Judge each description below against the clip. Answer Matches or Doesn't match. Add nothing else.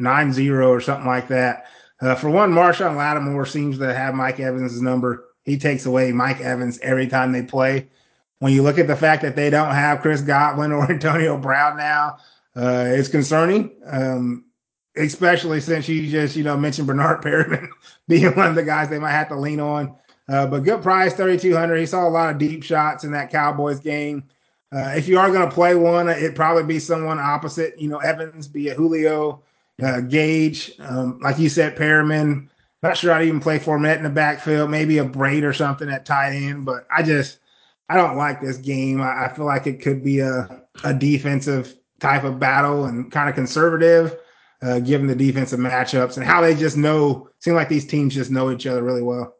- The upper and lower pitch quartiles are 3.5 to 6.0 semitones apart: Doesn't match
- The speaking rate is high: Matches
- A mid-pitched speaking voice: Matches